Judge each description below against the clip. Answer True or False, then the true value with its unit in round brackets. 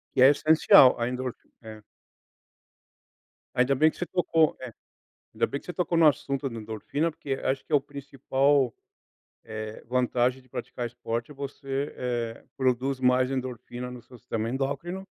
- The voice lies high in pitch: False (130 Hz)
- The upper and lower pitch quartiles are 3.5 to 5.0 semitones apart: False (2.6 semitones)